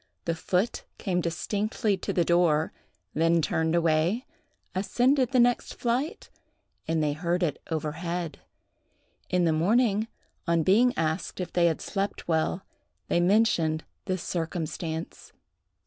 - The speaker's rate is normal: No, slow, 130 wpm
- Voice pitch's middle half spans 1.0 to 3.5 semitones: No, average, 3.9 semitones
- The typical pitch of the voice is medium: Yes, medium, 175 Hz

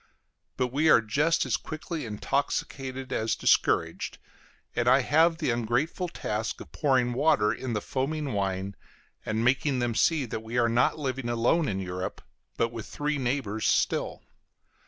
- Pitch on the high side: No, low, 125 Hz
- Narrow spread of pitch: No, average, 4.8 semitones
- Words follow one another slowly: No, average, 155 wpm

